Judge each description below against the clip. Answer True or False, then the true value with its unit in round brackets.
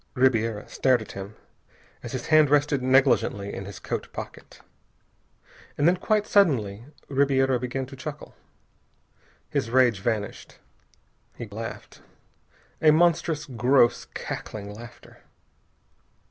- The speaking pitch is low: True (130 Hz)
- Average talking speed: False (115 wpm)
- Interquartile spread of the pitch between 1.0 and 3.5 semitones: False (4.4 semitones)